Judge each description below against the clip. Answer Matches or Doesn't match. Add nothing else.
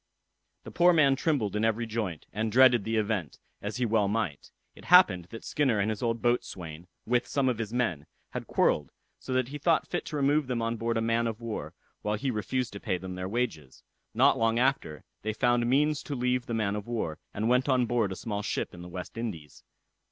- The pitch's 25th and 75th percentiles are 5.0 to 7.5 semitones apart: Doesn't match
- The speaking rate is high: Matches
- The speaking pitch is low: Matches